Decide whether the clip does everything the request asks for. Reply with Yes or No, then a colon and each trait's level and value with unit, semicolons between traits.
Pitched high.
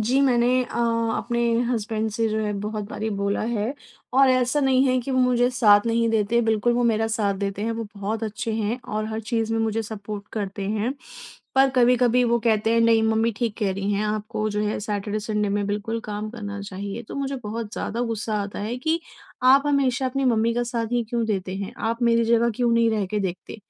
Yes: high, 225 Hz